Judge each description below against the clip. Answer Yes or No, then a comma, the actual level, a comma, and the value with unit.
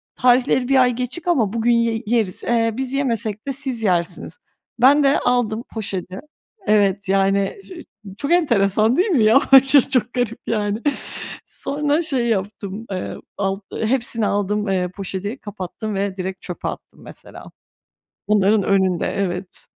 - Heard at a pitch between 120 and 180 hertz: No, high, 220 Hz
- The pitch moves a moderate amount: Yes, average, 4.2 semitones